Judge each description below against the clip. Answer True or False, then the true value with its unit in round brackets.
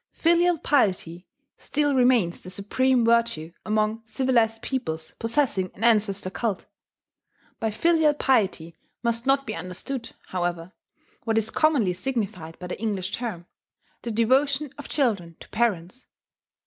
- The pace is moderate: False (130 wpm)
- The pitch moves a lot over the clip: True (6.0 semitones)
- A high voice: True (225 Hz)